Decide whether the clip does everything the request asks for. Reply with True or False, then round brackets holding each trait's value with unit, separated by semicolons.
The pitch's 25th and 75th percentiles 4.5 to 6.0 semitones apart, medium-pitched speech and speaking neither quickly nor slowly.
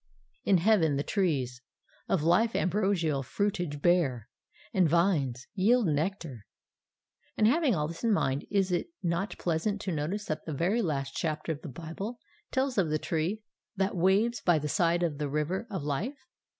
True (4.9 semitones; 170 Hz; 170 wpm)